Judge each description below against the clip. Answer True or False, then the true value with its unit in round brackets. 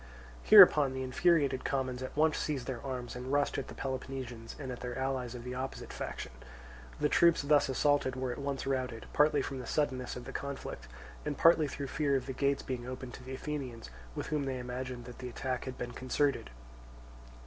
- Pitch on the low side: True (130 Hz)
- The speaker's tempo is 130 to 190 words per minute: False (205 wpm)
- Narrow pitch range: True (2.0 semitones)